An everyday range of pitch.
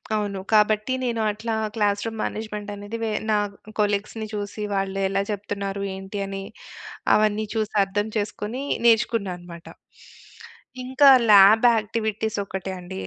No: narrow, 1.8 semitones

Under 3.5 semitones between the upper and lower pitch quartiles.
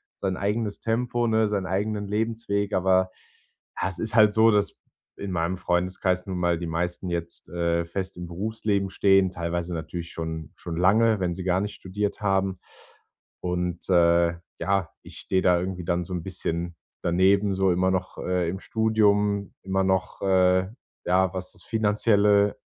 Yes: narrow, 2.6 semitones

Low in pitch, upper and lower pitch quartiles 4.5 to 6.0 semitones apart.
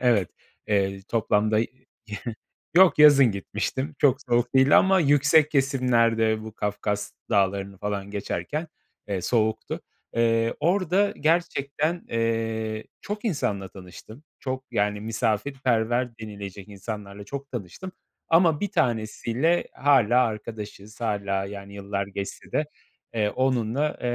Yes: low, 115 Hz; average, 5.2 semitones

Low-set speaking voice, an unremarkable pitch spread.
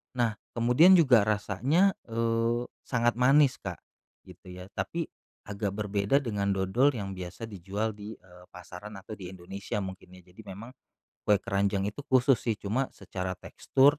Yes: low, 105 Hz; average, 4.0 semitones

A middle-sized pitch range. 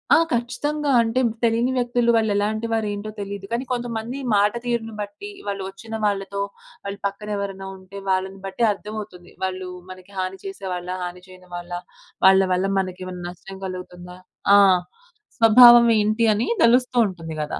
Yes: average, 3.6 semitones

